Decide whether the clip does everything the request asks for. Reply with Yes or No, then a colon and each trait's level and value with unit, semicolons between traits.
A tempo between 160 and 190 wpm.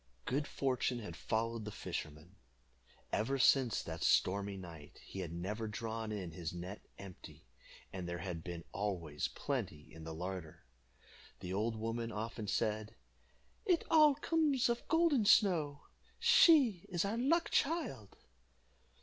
No: average, 140 wpm